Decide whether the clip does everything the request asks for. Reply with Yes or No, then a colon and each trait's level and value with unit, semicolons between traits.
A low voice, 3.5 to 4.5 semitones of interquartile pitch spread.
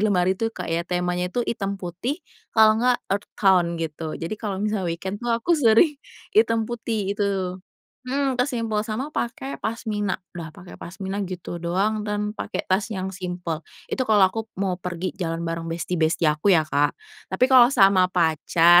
No: high, 195 Hz; average, 4.1 semitones